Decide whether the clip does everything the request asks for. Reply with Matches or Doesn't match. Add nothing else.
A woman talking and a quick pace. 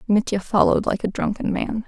Doesn't match